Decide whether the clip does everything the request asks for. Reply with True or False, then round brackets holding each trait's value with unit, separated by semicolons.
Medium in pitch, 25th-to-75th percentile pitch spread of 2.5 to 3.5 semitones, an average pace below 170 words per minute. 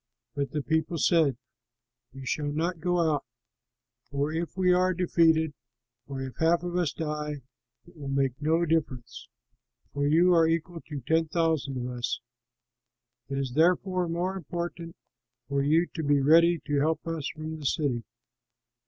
True (160 Hz; 3.0 semitones; 160 wpm)